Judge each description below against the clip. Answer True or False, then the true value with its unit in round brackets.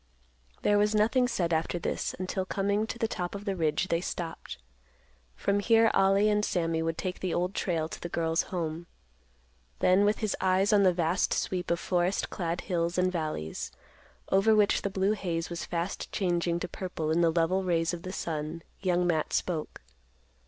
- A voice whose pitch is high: False (180 Hz)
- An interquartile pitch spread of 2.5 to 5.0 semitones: True (2.9 semitones)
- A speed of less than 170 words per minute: False (190 wpm)